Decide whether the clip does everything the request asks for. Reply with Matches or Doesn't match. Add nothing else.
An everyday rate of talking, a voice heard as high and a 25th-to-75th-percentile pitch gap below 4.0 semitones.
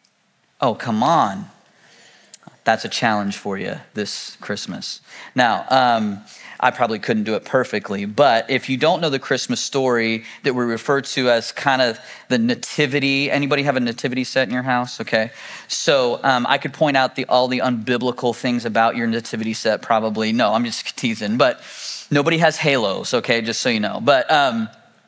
Doesn't match